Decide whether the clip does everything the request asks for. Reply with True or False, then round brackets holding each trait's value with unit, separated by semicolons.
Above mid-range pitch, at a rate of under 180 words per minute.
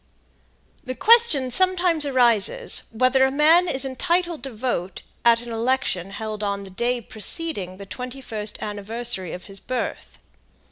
True (245 Hz; 145 wpm)